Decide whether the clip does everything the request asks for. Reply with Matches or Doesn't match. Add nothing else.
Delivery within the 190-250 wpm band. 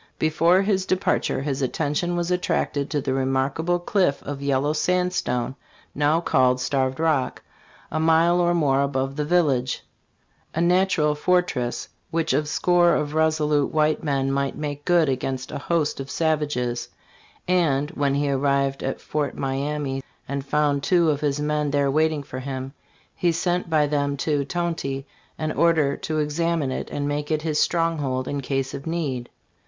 Doesn't match